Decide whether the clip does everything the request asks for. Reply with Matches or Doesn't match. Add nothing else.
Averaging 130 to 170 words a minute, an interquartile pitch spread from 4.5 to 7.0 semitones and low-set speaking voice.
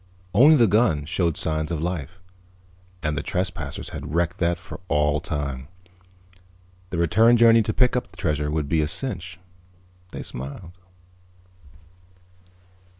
Matches